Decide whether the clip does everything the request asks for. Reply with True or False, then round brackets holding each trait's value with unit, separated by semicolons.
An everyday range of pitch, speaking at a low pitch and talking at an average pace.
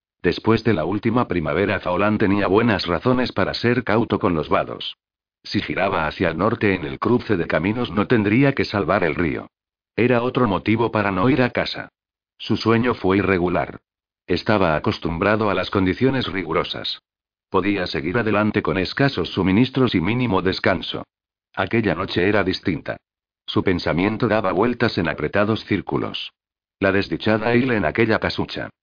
True (3.7 semitones; 105 Hz; 155 wpm)